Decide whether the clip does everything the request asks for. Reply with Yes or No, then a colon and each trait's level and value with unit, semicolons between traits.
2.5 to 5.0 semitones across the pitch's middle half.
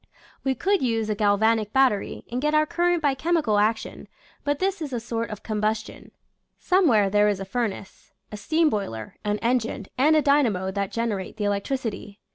No: wide, 5.6 semitones